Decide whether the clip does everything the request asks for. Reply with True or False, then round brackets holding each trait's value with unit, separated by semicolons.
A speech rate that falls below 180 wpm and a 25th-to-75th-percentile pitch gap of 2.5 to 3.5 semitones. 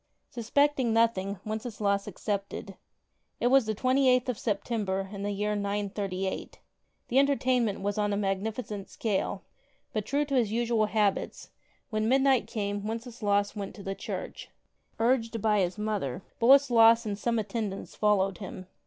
True (150 wpm; 2.8 semitones)